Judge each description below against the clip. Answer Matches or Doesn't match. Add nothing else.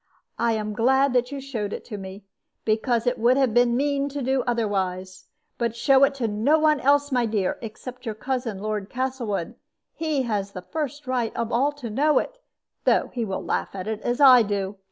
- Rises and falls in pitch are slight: Doesn't match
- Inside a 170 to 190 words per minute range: Doesn't match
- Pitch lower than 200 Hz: Doesn't match